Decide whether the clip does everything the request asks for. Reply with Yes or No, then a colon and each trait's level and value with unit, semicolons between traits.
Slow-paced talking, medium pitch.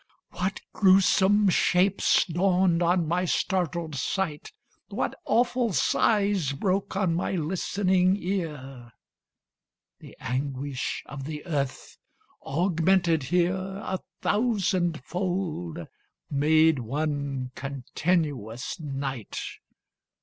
Yes: slow, 90 wpm; medium, 170 Hz